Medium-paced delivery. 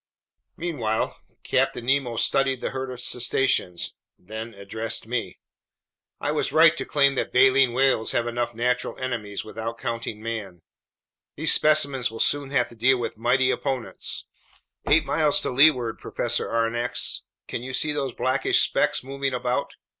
Yes: average, 150 wpm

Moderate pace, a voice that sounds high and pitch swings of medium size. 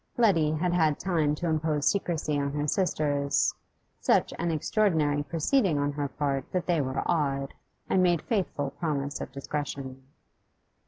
No: average, 150 wpm; medium, 150 Hz; average, 3.2 semitones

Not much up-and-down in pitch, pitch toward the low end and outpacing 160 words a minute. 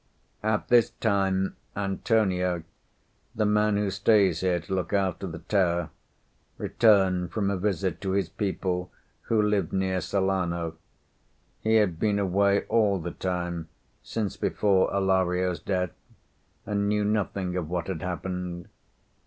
No: narrow, 2.2 semitones; very low, 95 Hz; slow, 135 wpm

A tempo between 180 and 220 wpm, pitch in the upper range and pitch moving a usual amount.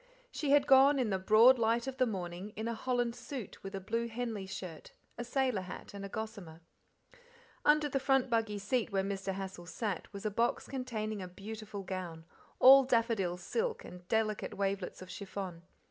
Yes: average, 185 wpm; high, 215 Hz; average, 4.2 semitones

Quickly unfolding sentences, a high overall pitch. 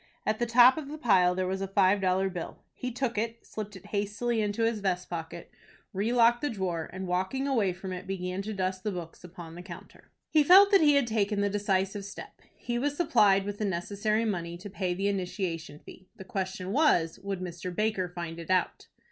Yes: fast, 215 wpm; high, 195 Hz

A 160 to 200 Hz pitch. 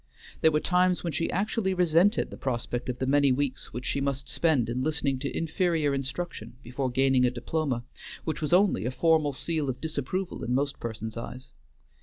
No: medium, 140 Hz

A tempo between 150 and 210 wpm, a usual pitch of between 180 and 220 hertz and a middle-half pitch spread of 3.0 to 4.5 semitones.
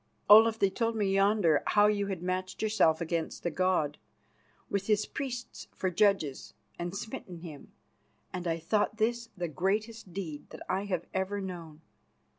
Yes: average, 160 wpm; high, 190 Hz; average, 3.7 semitones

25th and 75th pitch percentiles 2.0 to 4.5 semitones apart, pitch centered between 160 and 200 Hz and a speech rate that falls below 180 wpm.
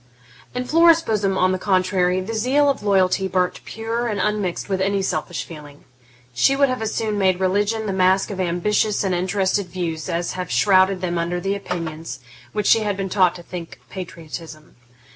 No: average, 2.8 semitones; high, 190 Hz; average, 185 wpm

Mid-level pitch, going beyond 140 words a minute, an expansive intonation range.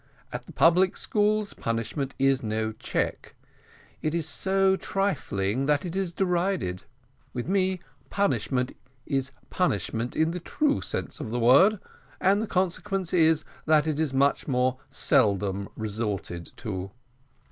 No: medium, 150 Hz; slow, 135 wpm; wide, 8.3 semitones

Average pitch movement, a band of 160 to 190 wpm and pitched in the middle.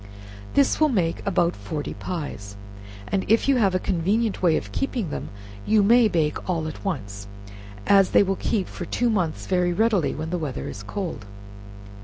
Yes: average, 5.0 semitones; average, 180 wpm; medium, 180 Hz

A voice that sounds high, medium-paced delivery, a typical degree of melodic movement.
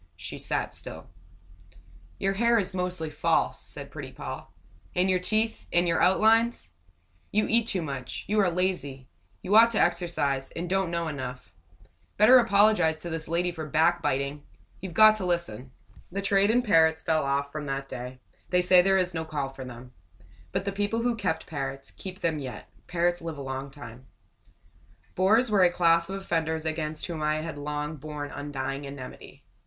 No: medium, 165 Hz; average, 180 wpm; average, 5.0 semitones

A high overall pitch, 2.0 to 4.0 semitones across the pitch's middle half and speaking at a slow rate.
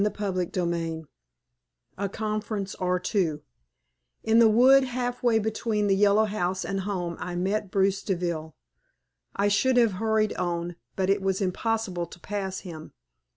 No: high, 195 Hz; average, 3.2 semitones; average, 150 wpm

